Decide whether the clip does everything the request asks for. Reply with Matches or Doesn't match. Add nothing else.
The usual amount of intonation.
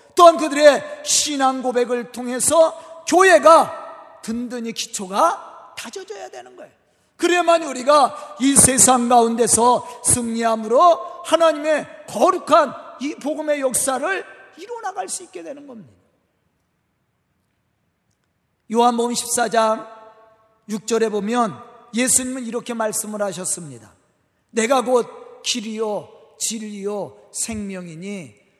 Doesn't match